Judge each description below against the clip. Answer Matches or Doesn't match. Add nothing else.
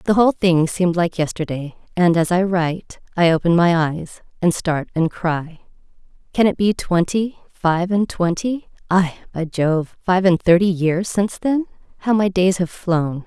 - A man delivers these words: Doesn't match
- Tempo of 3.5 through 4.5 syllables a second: Matches